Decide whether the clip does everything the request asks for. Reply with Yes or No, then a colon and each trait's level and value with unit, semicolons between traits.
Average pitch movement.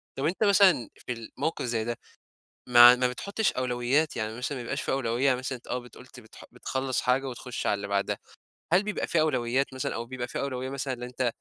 No: narrow, 2.2 semitones